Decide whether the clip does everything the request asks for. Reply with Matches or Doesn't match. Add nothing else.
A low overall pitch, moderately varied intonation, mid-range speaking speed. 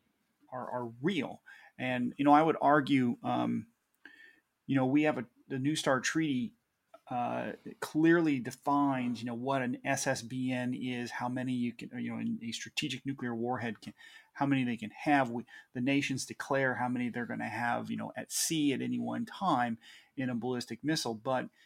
Matches